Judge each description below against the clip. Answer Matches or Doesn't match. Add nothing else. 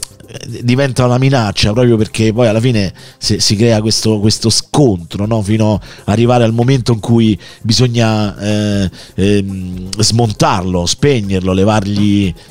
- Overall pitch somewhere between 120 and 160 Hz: Doesn't match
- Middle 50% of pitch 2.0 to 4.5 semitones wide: Matches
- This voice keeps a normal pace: Matches